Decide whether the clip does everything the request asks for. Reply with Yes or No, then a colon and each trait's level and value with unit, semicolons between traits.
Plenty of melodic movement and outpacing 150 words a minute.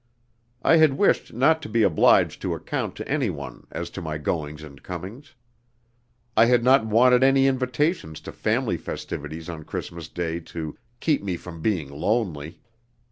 Yes: wide, 8.0 semitones; average, 160 wpm